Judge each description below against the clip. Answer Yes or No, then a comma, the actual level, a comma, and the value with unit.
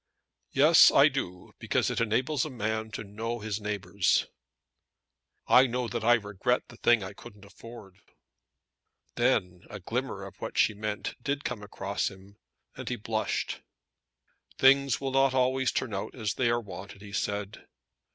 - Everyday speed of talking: Yes, average, 160 wpm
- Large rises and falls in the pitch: No, average, 3.8 semitones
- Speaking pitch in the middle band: No, low, 110 Hz